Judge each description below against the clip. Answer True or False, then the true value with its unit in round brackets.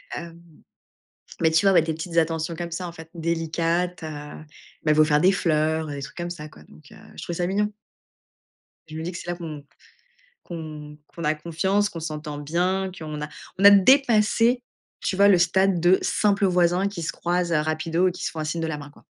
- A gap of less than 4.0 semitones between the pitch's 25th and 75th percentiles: True (2.7 semitones)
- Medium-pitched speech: True (170 Hz)